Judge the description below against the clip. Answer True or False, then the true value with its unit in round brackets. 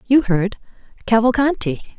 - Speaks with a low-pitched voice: False (230 Hz)